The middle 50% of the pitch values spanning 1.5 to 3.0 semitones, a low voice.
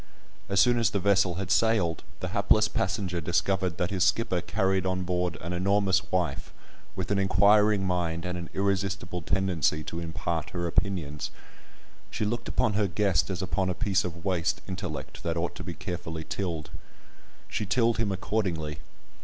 Yes: narrow, 2.5 semitones; very low, 95 Hz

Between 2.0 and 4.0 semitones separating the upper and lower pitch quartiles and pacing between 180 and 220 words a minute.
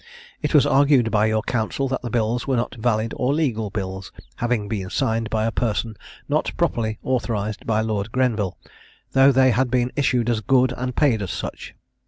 Yes: average, 2.8 semitones; average, 190 wpm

